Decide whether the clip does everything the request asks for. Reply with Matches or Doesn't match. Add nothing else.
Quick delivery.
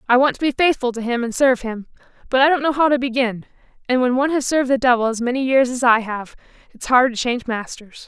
Matches